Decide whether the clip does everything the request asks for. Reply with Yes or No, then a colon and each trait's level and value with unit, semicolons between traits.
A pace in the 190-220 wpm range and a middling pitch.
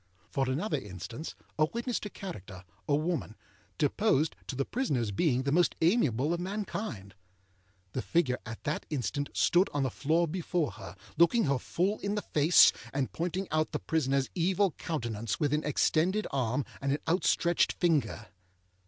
No: average, 160 wpm; medium, 155 Hz